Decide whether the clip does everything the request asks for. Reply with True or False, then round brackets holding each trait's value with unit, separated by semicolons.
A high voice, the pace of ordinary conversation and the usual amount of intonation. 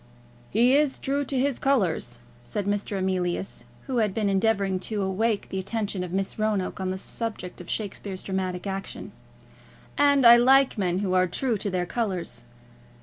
True (200 Hz; 170 wpm; 3.9 semitones)